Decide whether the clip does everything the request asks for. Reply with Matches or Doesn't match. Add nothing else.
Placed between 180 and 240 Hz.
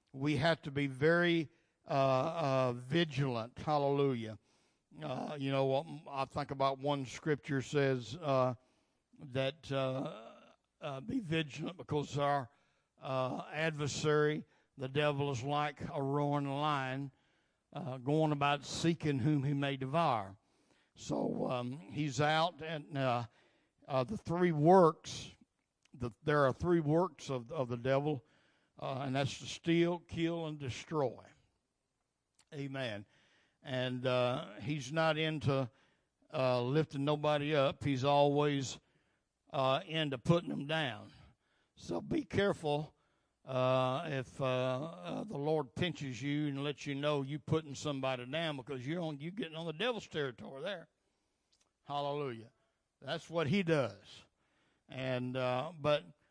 Doesn't match